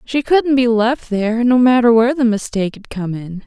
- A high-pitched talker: Yes, high, 235 Hz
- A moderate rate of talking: No, fast, 225 wpm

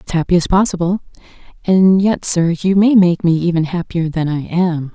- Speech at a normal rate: Yes, average, 195 wpm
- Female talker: Yes, female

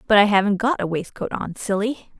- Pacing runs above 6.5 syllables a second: No, 5.5 syllables/s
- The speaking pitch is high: Yes, high, 205 Hz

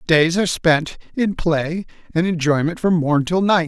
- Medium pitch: Yes, medium, 170 Hz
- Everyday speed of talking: Yes, average, 180 wpm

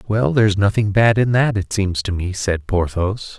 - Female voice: No, male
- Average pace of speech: No, fast, 215 wpm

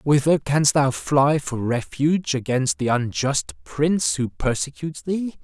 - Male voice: Yes, male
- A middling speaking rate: Yes, average, 145 wpm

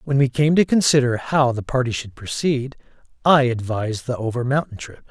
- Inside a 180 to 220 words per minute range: Yes, average, 190 wpm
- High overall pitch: No, low, 125 Hz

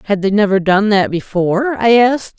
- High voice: Yes, high, 210 Hz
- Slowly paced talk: No, average, 200 wpm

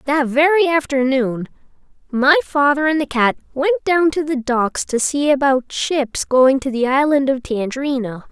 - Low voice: No, very high, 275 Hz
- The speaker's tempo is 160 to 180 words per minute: Yes, average, 165 wpm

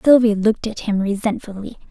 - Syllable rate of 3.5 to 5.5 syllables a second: No, 5.9 syllables/s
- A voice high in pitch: Yes, high, 215 Hz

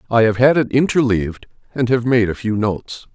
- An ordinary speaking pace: No, fast, 210 wpm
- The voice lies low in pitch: Yes, low, 115 Hz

